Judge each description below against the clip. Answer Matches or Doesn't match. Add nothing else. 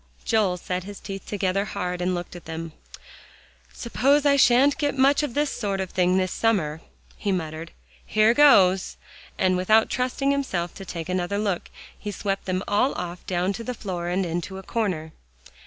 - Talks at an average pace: Matches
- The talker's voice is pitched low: Doesn't match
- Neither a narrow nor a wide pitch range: Matches